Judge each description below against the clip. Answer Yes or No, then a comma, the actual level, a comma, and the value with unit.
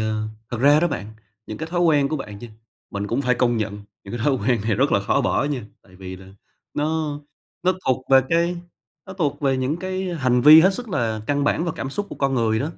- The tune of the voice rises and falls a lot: Yes, wide, 5.8 semitones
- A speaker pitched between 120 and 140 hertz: Yes, low, 135 Hz